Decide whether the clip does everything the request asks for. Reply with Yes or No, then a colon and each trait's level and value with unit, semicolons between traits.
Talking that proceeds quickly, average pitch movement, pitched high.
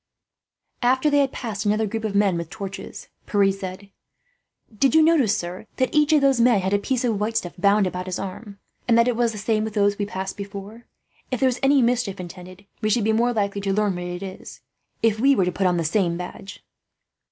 Yes: fast, 230 wpm; average, 3.6 semitones; high, 205 Hz